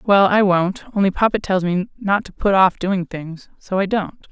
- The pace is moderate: No, fast, 220 wpm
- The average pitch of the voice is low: No, high, 190 Hz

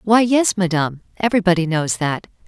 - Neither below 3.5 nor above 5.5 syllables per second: No, 5.8 syllables/s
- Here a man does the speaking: No, female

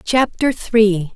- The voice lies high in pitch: Yes, high, 215 Hz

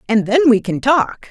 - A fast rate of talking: Yes, fast, 230 wpm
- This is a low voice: No, high, 240 Hz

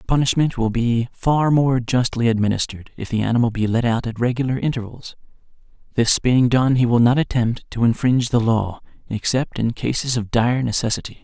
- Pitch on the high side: No, low, 120 Hz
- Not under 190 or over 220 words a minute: No, average, 180 wpm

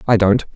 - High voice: No, low, 100 Hz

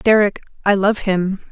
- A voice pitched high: Yes, high, 200 Hz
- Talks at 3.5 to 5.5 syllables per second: Yes, 4.2 syllables/s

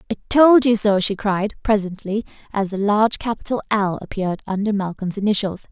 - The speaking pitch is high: Yes, high, 205 Hz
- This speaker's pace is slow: No, average, 170 wpm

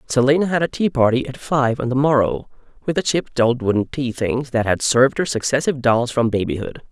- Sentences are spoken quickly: Yes, fast, 215 wpm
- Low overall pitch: Yes, low, 130 Hz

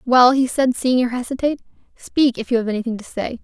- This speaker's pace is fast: Yes, fast, 225 wpm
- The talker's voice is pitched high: Yes, high, 245 Hz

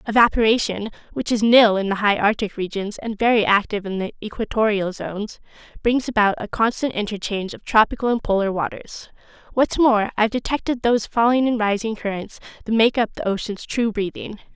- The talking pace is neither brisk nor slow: Yes, average, 170 wpm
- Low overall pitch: No, high, 215 Hz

